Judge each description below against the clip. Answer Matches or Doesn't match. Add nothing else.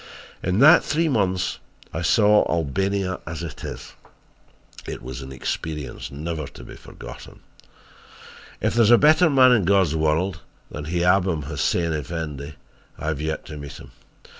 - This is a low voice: Matches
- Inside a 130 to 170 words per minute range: Matches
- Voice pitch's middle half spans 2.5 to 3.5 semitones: Doesn't match